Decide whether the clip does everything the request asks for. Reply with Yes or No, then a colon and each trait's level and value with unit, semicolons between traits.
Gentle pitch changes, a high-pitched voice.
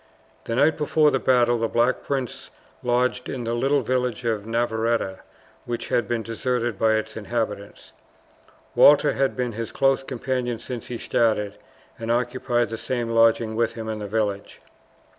No: narrow, 2.0 semitones; low, 120 Hz